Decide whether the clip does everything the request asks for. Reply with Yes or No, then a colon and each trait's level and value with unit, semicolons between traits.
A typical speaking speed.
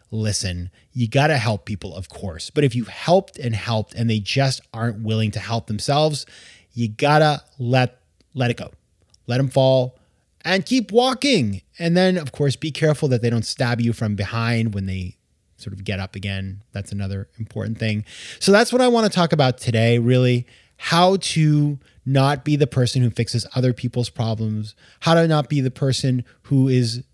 Yes: average, 195 wpm